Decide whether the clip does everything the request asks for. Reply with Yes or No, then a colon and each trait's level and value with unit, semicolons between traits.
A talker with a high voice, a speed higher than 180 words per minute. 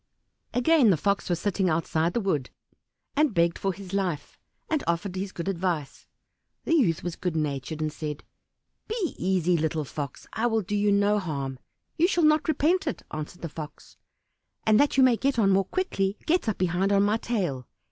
Yes: high, 195 Hz; average, 190 wpm